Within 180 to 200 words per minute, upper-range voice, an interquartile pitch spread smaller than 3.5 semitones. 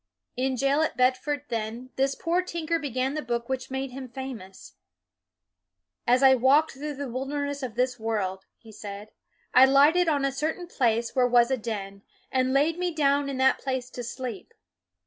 Yes: average, 190 wpm; very high, 260 Hz; average, 3.0 semitones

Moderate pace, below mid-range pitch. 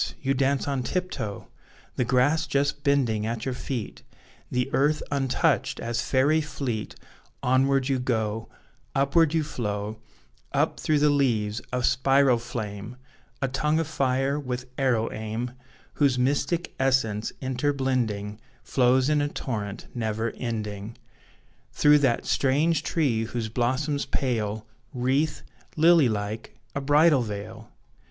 No: slow, 130 wpm; low, 130 Hz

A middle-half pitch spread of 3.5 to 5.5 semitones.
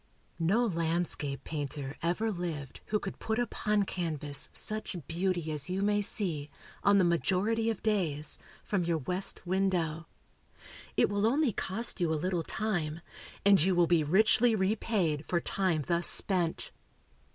Yes: average, 4.1 semitones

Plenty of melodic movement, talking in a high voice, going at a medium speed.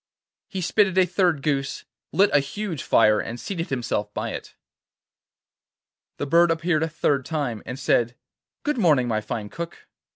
No: wide, 5.7 semitones; medium, 155 Hz; average, 160 wpm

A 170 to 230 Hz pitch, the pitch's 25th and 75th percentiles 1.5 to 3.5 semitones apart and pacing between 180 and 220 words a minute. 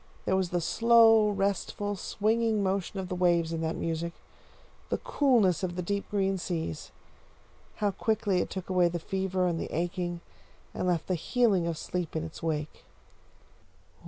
No: medium, 185 Hz; average, 3.1 semitones; average, 165 wpm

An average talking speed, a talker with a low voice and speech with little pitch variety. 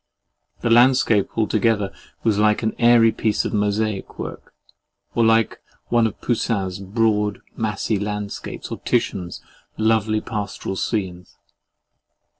No: slow, 115 wpm; low, 110 Hz; narrow, 1.8 semitones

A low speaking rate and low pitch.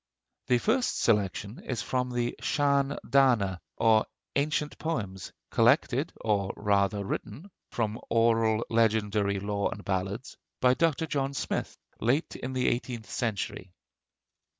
Yes: slow, 125 wpm; low, 115 Hz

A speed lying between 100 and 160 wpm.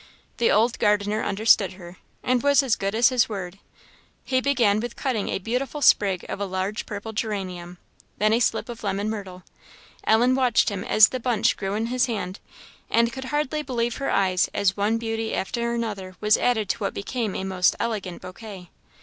No: average, 190 wpm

